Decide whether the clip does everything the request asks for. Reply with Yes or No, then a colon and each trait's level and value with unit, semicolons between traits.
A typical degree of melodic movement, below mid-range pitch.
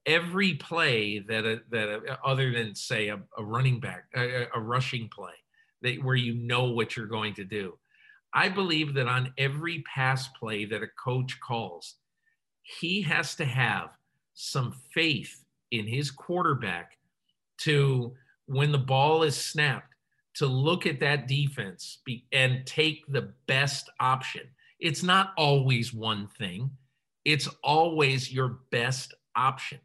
Yes: average, 3.9 semitones; low, 130 Hz